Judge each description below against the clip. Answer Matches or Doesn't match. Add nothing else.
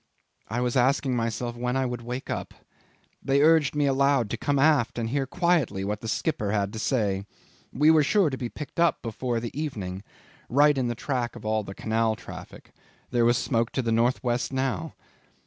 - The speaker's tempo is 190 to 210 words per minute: Matches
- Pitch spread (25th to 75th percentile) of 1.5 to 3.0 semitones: Doesn't match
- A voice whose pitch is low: Matches